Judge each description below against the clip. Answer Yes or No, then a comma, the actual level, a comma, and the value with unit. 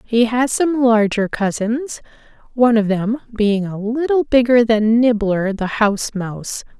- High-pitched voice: Yes, high, 225 Hz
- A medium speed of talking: Yes, average, 150 wpm